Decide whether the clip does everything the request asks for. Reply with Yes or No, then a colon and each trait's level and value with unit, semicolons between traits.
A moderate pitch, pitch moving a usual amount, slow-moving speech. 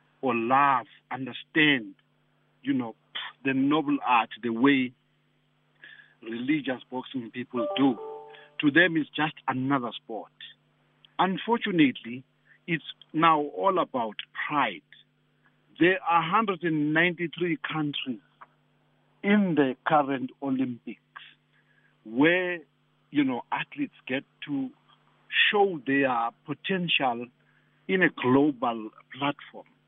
No: medium, 150 Hz; wide, 6.6 semitones; slow, 95 wpm